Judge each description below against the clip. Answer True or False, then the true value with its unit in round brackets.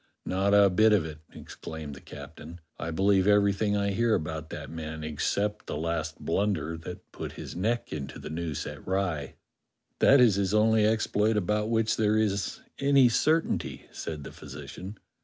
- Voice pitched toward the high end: False (100 Hz)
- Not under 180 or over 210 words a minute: False (170 wpm)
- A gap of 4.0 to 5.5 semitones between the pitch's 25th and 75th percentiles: True (4.9 semitones)